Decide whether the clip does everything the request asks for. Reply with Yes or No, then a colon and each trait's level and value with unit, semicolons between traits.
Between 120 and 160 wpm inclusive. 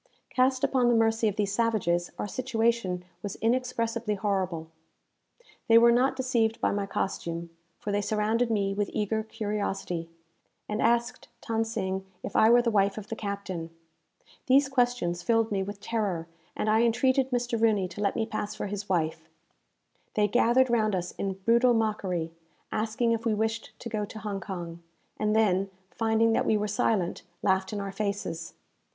No: average, 170 wpm